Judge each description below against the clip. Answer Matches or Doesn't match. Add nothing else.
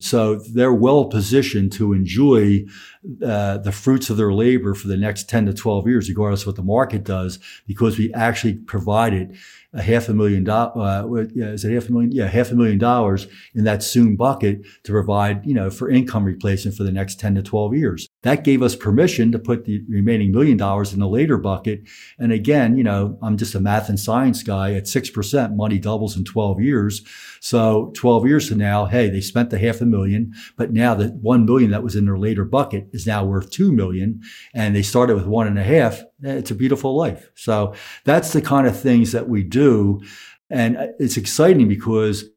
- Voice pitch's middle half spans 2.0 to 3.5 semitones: Matches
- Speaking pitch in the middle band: Doesn't match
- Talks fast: Matches